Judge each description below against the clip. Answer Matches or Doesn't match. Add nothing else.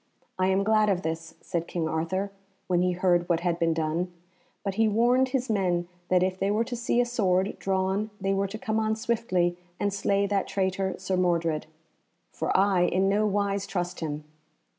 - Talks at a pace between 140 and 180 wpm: Doesn't match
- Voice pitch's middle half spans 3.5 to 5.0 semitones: Doesn't match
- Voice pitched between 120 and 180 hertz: Doesn't match